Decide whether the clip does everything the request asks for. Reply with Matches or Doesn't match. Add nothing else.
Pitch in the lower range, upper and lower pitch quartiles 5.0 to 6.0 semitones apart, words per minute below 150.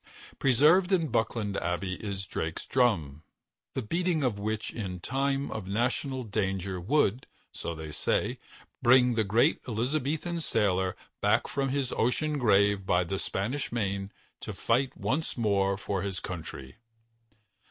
Matches